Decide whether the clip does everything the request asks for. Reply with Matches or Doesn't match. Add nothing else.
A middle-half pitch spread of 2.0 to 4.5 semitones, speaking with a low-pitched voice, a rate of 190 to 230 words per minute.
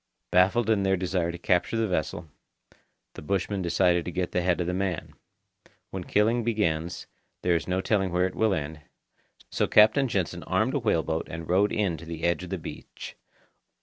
Matches